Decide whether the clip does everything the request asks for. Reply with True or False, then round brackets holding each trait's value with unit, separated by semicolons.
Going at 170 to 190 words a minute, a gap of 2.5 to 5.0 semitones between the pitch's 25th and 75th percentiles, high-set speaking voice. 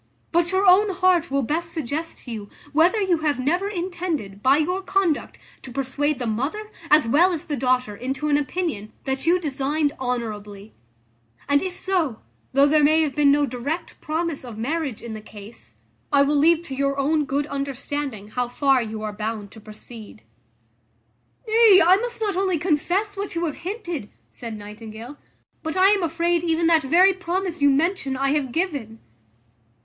False (180 wpm; 5.5 semitones; 295 Hz)